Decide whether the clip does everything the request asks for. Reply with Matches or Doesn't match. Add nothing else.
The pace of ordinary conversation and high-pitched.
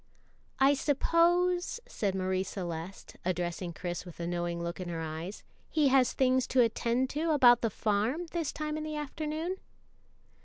Matches